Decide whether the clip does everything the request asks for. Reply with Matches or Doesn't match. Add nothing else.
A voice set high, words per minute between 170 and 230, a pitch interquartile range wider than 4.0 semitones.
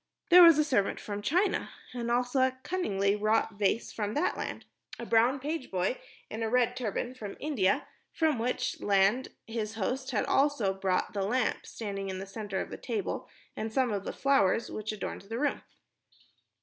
Matches